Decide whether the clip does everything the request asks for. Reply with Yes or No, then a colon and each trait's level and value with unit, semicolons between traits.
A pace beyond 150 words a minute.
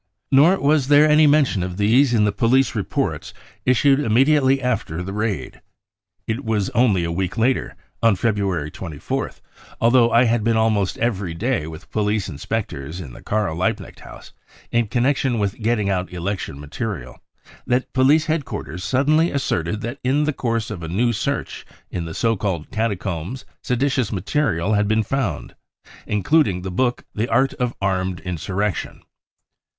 Yes: average, 160 wpm